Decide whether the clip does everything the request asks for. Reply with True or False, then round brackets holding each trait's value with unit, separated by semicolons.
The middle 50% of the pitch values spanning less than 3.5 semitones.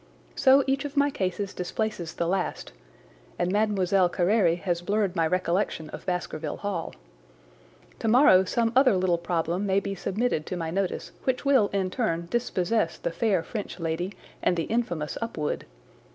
False (4.1 semitones)